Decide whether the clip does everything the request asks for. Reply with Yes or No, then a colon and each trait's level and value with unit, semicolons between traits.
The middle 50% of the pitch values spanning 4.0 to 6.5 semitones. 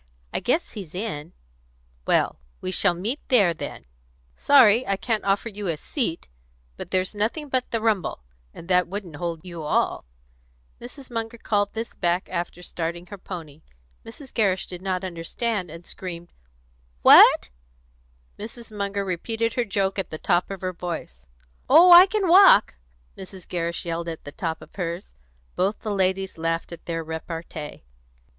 Yes: average, 4.6 semitones